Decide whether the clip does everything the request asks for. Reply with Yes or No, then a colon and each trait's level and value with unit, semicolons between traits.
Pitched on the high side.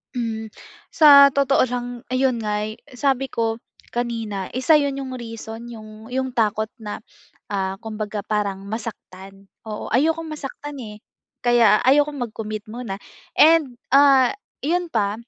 Yes: high, 235 Hz